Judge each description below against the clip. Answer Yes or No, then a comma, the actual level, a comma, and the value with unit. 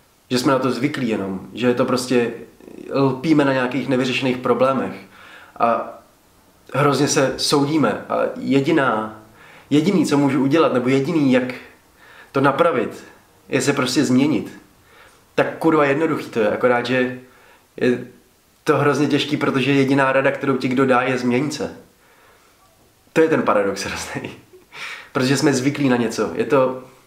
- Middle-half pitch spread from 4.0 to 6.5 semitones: No, narrow, 2.4 semitones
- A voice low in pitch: Yes, low, 130 Hz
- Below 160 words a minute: Yes, average, 145 wpm